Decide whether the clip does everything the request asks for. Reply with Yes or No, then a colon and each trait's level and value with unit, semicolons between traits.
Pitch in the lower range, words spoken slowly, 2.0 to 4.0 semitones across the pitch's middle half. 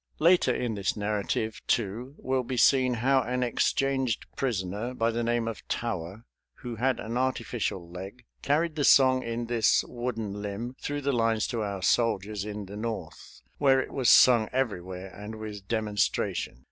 No: low, 115 Hz; average, 165 wpm; average, 3.6 semitones